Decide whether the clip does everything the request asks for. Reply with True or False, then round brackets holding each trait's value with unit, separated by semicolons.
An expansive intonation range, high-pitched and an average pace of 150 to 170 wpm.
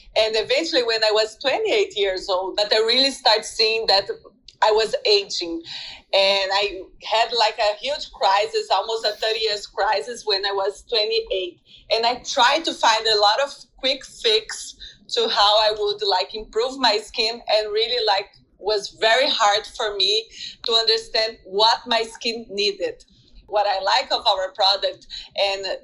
True (6.1 semitones; 225 Hz; 165 wpm)